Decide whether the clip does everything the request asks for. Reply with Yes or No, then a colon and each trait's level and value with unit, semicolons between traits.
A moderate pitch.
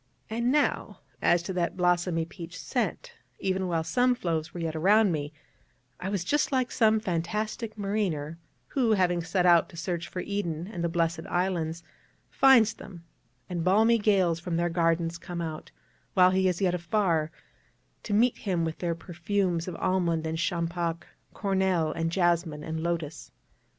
Yes: medium, 175 Hz